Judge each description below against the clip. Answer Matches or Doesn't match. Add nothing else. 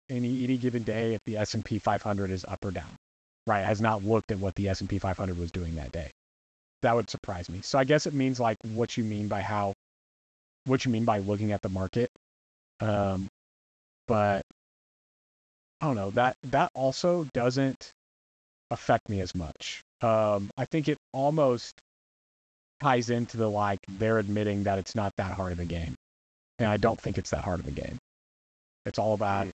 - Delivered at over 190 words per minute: Matches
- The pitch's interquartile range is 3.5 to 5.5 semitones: Matches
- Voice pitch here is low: Matches